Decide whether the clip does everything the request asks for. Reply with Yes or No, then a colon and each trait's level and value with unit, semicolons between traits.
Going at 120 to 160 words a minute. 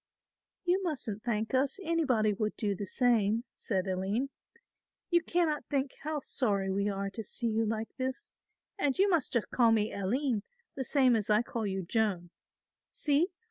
No: average, 170 wpm